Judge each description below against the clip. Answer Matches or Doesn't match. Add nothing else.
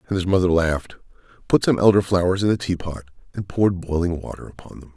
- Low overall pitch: Matches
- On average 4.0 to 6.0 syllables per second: Doesn't match